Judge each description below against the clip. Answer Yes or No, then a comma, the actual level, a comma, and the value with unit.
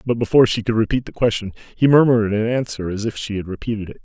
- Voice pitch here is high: No, low, 110 Hz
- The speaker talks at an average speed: No, fast, 250 wpm